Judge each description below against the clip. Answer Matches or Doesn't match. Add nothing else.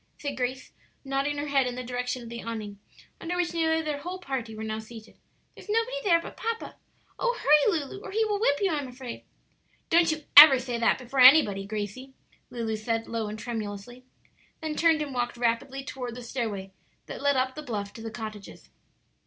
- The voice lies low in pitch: Doesn't match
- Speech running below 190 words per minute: Doesn't match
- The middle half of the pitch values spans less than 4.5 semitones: Doesn't match